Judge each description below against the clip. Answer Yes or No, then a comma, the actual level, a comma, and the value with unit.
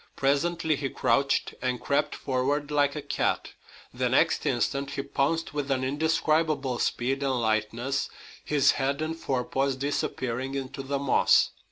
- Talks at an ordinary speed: Yes, average, 145 wpm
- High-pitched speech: No, medium, 140 Hz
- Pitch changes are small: Yes, narrow, 1.9 semitones